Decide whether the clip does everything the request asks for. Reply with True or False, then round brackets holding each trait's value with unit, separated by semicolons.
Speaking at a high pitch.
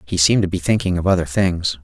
False (90 Hz)